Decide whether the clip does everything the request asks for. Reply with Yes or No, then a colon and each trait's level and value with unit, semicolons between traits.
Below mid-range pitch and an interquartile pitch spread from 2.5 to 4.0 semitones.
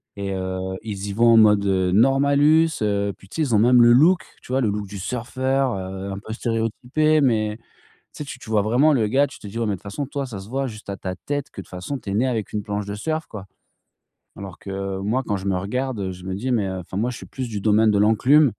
No: low, 110 Hz; average, 4.8 semitones